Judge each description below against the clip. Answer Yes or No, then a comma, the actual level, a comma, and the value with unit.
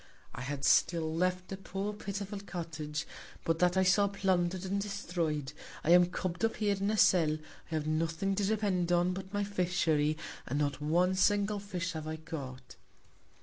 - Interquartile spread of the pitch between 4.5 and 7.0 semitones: No, average, 3.8 semitones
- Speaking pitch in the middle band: Yes, medium, 180 Hz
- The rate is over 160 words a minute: Yes, average, 180 wpm